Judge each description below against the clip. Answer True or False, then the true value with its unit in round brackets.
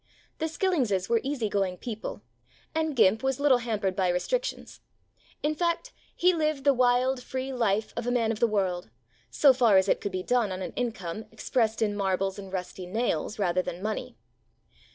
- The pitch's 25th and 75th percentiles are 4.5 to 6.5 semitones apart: True (5.4 semitones)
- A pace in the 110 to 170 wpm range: False (190 wpm)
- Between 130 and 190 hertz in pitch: False (225 Hz)